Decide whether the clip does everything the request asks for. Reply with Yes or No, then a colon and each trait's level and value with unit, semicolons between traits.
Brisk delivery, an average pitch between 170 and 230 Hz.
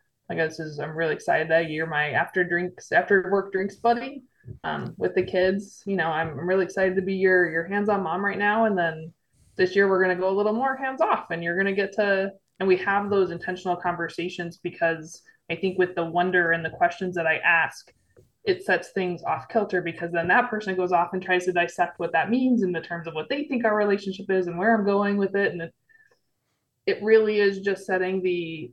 Yes: fast, 235 wpm; medium, 185 Hz